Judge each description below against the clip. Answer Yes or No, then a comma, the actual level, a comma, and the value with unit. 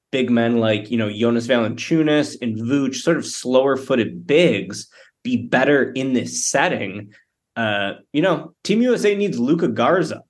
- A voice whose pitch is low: Yes, low, 130 Hz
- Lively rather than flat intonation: Yes, wide, 6.2 semitones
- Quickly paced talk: No, average, 155 wpm